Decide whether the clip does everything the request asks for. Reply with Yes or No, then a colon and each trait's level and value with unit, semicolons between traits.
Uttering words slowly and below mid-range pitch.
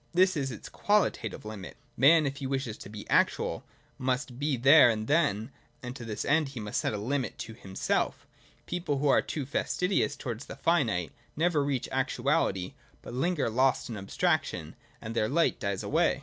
No: average, 185 wpm; low, 130 Hz